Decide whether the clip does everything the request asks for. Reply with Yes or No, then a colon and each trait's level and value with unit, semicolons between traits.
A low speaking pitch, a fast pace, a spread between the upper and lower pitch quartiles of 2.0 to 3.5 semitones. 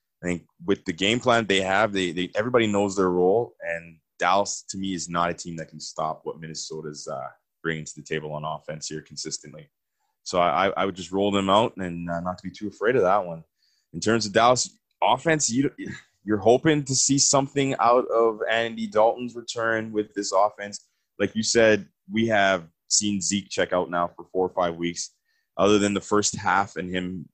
No: low, 100 Hz; fast, 210 wpm; average, 4.8 semitones